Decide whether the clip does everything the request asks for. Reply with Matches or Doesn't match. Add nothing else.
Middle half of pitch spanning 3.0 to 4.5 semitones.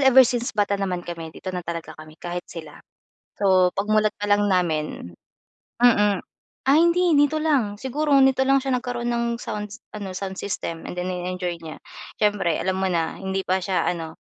Doesn't match